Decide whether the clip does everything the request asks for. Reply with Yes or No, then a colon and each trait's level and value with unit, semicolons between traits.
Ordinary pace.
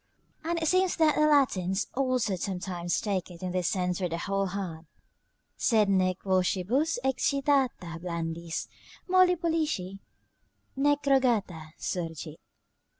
No: slow, 125 wpm